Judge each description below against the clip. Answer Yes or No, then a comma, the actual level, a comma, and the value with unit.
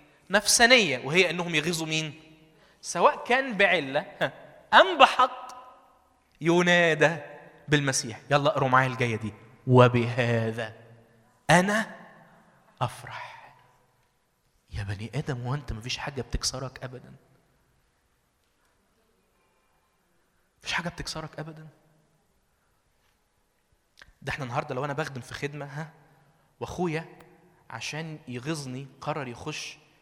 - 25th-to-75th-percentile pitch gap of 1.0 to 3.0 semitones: No, average, 4.9 semitones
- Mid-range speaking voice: Yes, medium, 150 Hz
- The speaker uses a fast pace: No, average, 95 wpm